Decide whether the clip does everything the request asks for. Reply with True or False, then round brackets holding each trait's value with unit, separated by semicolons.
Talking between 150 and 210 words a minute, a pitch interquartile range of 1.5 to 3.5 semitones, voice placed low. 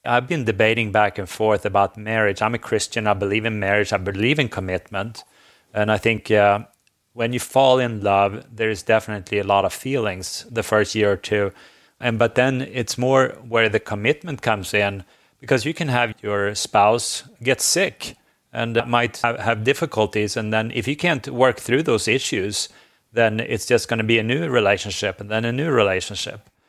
True (195 wpm; 2.7 semitones; 110 Hz)